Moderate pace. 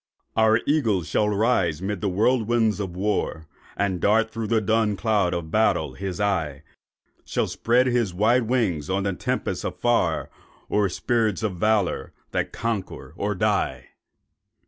Yes: average, 145 wpm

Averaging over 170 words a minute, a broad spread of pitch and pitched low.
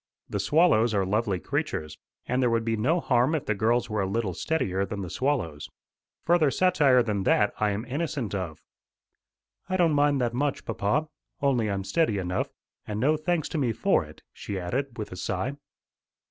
Yes: average, 190 wpm; wide, 6.3 semitones; low, 115 Hz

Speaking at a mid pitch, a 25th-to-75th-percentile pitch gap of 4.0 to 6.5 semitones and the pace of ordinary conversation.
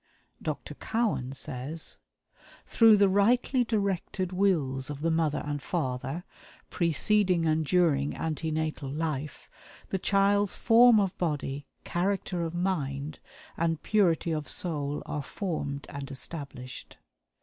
No: medium, 165 Hz; average, 5.2 semitones; slow, 120 wpm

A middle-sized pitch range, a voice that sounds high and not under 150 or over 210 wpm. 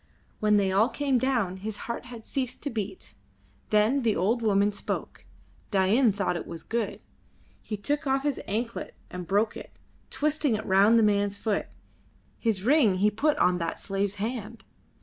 Yes: average, 3.5 semitones; high, 215 Hz; average, 170 wpm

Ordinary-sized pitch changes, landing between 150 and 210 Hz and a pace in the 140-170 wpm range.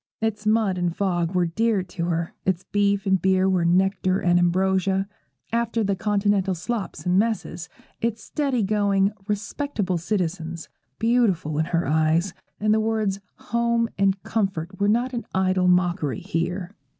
Yes: average, 3.2 semitones; high, 190 Hz; average, 150 wpm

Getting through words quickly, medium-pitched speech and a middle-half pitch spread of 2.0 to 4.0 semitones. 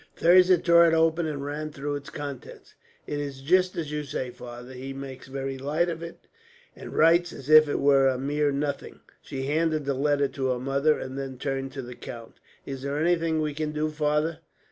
Yes: fast, 210 wpm; medium, 145 Hz; narrow, 2.6 semitones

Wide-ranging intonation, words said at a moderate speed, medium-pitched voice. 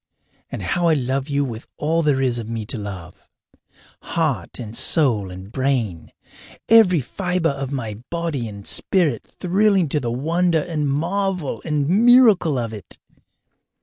Yes: wide, 6.5 semitones; average, 150 wpm; medium, 145 Hz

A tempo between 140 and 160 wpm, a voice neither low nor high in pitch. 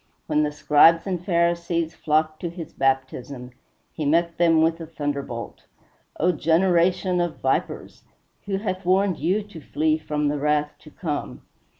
Yes: average, 155 wpm; medium, 165 Hz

